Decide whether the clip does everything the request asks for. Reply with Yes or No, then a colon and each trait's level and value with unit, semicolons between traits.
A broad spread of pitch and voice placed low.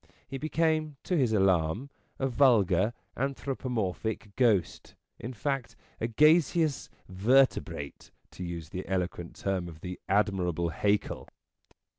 Yes: wide, 6.8 semitones; low, 110 Hz